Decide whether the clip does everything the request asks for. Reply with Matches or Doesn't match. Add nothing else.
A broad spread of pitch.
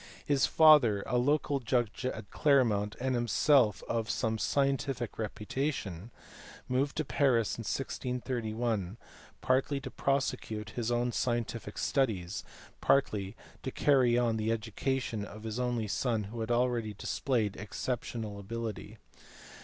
Doesn't match